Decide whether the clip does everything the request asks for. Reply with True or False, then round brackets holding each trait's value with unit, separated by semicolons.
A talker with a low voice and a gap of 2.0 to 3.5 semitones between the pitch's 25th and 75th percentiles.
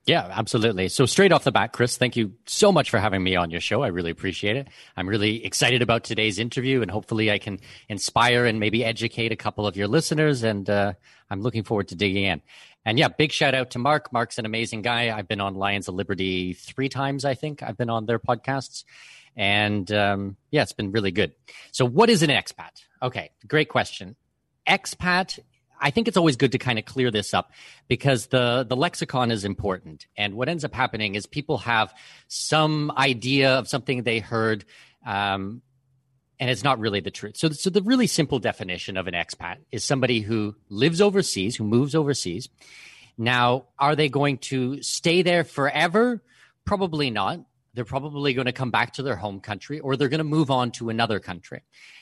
False (120 Hz; 4.9 semitones)